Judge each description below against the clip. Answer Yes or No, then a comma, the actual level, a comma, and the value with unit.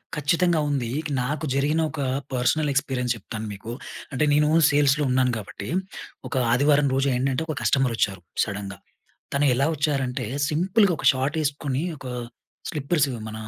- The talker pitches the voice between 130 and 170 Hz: Yes, medium, 140 Hz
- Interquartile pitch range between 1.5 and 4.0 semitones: Yes, average, 3.2 semitones